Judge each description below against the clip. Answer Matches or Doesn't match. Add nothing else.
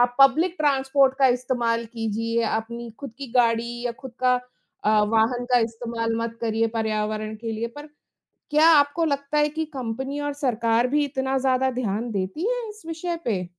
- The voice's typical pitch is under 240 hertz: Doesn't match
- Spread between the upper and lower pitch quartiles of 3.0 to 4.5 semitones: Matches